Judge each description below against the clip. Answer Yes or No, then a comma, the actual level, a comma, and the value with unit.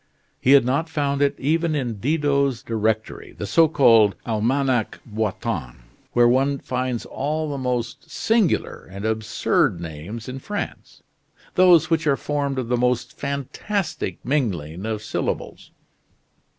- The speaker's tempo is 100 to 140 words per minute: Yes, slow, 135 wpm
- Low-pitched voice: Yes, low, 130 Hz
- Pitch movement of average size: Yes, average, 4.6 semitones